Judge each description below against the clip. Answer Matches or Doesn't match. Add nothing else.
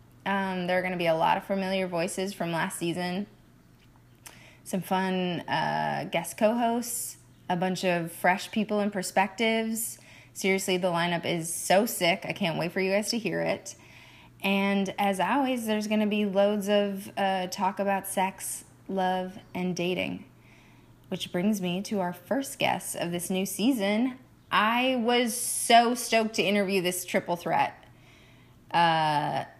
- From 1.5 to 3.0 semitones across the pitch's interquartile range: Matches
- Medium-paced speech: Matches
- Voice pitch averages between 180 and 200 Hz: Matches